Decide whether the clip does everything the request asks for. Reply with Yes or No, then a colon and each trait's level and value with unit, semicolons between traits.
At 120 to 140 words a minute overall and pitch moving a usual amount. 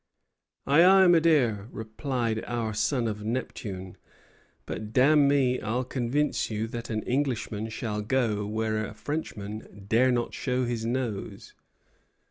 Yes: slow, 135 wpm; average, 3.3 semitones